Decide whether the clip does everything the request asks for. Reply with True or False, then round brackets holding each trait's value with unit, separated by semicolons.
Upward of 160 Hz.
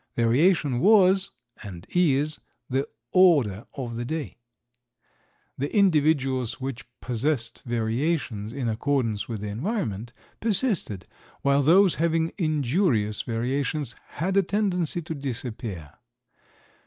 False (140 Hz)